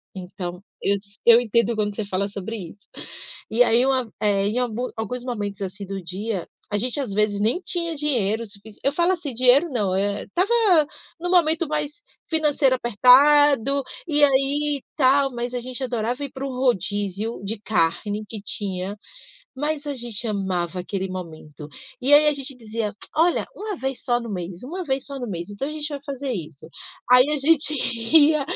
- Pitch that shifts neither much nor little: No, wide, 5.7 semitones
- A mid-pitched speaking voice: No, high, 240 Hz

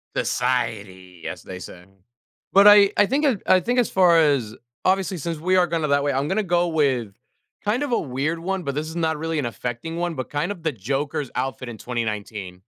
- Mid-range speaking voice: Yes, medium, 150 Hz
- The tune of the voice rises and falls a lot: Yes, wide, 6.6 semitones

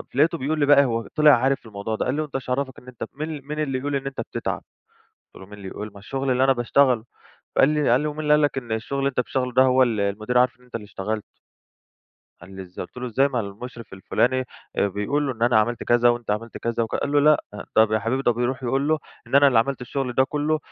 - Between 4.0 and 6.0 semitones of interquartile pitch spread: No, average, 3.5 semitones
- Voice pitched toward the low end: Yes, low, 125 Hz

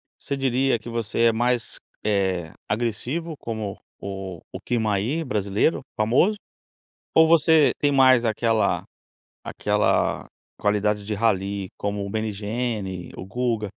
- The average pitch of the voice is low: Yes, low, 110 Hz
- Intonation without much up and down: No, average, 3.6 semitones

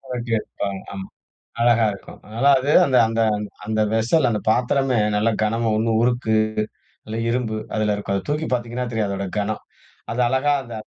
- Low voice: Yes, low, 115 Hz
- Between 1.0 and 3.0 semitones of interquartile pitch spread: Yes, narrow, 2.5 semitones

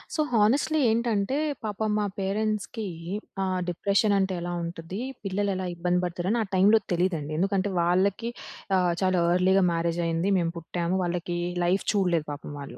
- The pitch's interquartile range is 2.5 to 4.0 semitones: Yes, average, 2.9 semitones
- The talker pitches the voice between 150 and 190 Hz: Yes, medium, 185 Hz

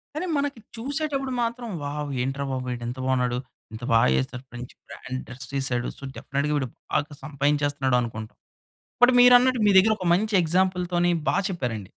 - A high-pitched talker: No, medium, 145 Hz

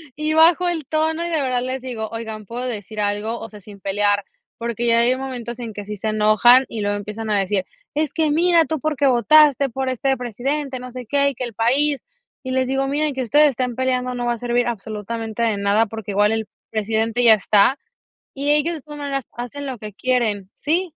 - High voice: Yes, high, 245 Hz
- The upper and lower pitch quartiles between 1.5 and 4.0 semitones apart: No, average, 4.4 semitones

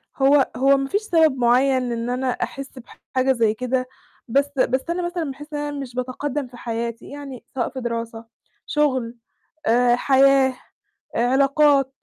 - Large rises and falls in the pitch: No, narrow, 2.4 semitones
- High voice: Yes, very high, 265 Hz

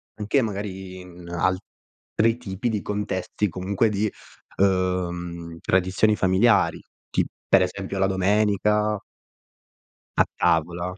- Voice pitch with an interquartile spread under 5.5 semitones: Yes, narrow, 2.4 semitones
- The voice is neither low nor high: No, very low, 95 Hz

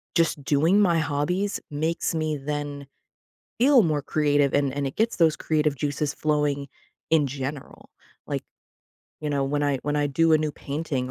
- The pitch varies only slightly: Yes, narrow, 2.1 semitones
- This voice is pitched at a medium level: Yes, medium, 150 Hz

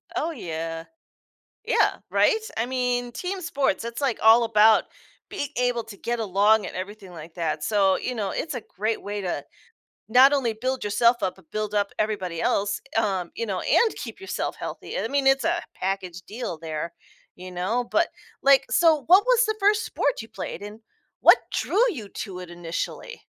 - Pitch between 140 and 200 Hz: No, high, 220 Hz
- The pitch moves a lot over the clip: Yes, wide, 6.0 semitones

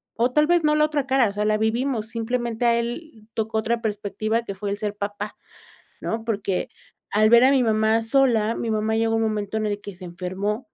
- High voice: Yes, high, 220 Hz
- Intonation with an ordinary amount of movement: No, narrow, 2.2 semitones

